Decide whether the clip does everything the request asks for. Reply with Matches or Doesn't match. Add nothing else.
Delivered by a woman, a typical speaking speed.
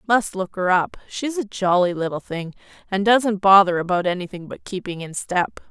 Matches